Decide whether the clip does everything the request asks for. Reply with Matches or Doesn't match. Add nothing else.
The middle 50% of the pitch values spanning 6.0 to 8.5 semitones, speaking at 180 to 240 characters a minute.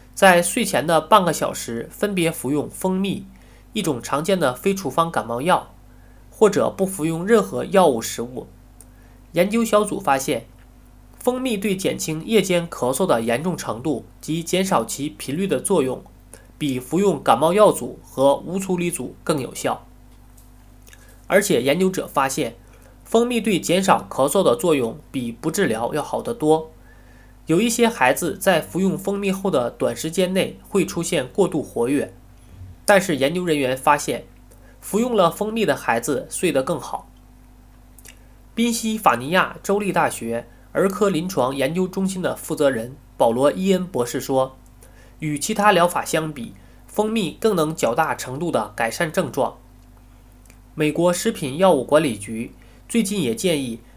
Matches